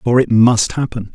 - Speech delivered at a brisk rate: Yes, fast, 210 wpm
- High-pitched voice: No, low, 115 Hz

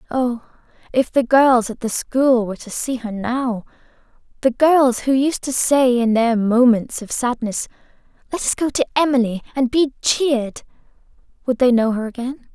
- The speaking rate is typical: Yes, average, 165 wpm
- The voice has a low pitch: No, very high, 250 Hz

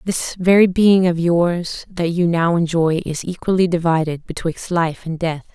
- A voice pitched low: No, medium, 170 Hz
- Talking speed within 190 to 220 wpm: No, average, 175 wpm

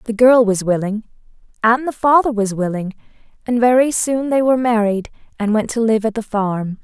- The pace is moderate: Yes, average, 195 wpm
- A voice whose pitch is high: Yes, high, 225 Hz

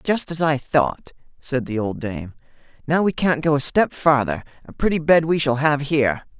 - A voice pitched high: No, medium, 145 Hz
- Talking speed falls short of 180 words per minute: No, fast, 205 wpm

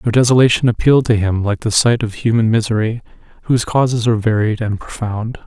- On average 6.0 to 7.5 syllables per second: Yes, 6.1 syllables/s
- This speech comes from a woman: No, male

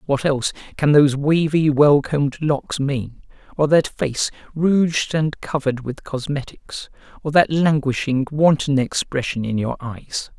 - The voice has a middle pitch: Yes, medium, 145 Hz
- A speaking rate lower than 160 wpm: Yes, average, 145 wpm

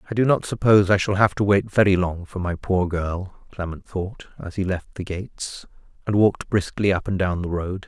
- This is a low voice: Yes, very low, 95 Hz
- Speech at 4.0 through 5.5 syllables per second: Yes, 5.2 syllables/s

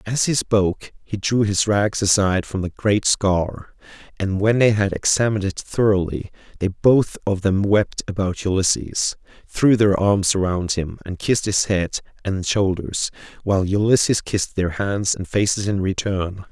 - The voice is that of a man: Yes, male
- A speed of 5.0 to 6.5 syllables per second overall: No, 4.5 syllables/s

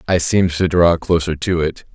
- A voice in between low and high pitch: No, very low, 85 Hz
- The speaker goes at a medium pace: No, fast, 215 wpm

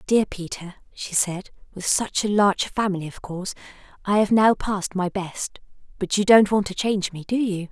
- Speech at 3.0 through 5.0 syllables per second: No, 5.2 syllables/s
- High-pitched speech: Yes, high, 195 Hz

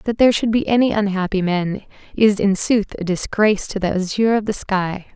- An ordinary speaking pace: No, fast, 210 wpm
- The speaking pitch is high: Yes, high, 205 Hz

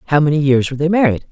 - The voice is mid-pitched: Yes, medium, 150 Hz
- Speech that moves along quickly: Yes, fast, 275 wpm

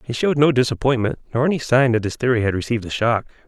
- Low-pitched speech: Yes, low, 125 Hz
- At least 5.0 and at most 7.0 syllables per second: No, 7.2 syllables/s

